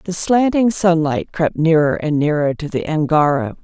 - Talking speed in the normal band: Yes, average, 165 wpm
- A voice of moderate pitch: Yes, medium, 160 Hz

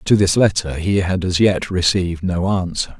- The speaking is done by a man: Yes, male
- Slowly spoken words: No, average, 200 wpm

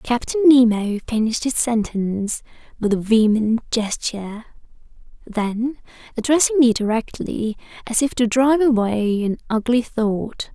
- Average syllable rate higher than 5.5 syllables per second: No, 4.5 syllables/s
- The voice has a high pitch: Yes, high, 230 Hz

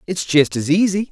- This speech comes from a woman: No, male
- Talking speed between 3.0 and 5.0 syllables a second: No, 5.2 syllables/s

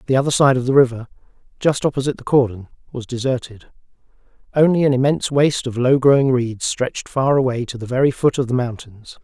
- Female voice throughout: No, male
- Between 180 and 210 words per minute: Yes, average, 195 wpm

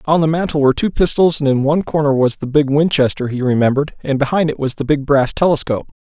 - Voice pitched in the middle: Yes, medium, 145 Hz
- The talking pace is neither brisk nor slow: No, fast, 240 wpm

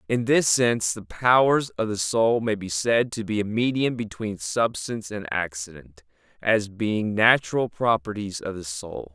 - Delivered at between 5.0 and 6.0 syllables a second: No, 4.4 syllables/s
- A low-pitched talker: Yes, low, 105 Hz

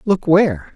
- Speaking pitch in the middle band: Yes, medium, 170 Hz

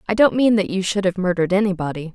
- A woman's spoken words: Yes, female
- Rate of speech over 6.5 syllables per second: Yes, 7.0 syllables/s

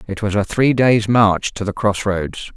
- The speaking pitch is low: Yes, low, 105 Hz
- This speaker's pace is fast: Yes, fast, 235 wpm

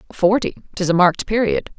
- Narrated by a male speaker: No, female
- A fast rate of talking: No, average, 170 wpm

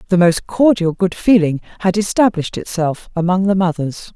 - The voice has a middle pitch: Yes, medium, 180 Hz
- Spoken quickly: No, average, 160 wpm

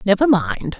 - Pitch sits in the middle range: No, high, 220 Hz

